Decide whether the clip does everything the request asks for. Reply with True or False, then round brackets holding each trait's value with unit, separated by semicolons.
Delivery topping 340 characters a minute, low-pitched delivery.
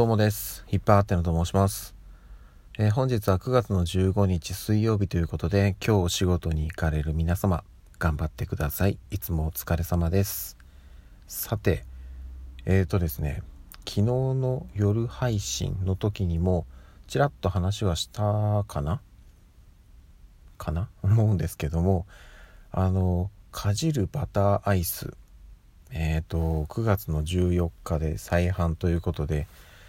False (260 characters per minute; 90 Hz)